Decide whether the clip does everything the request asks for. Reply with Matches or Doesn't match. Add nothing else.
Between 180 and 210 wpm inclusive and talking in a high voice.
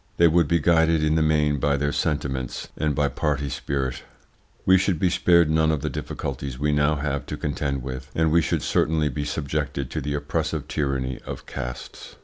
Doesn't match